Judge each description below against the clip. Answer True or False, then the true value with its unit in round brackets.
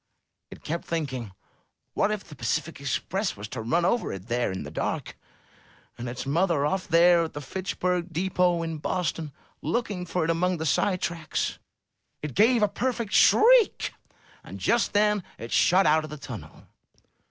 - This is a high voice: False (170 Hz)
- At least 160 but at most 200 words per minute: True (170 wpm)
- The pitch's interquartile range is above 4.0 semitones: True (4.5 semitones)